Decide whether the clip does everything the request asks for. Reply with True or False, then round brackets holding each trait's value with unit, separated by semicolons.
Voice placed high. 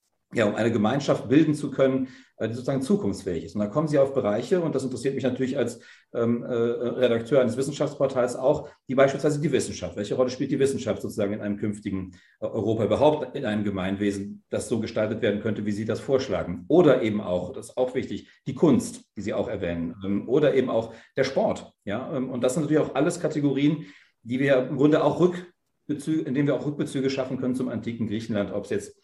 False (130 Hz)